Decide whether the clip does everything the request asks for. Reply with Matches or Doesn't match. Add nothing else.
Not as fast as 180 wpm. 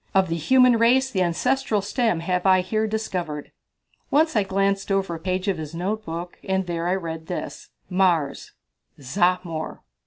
Matches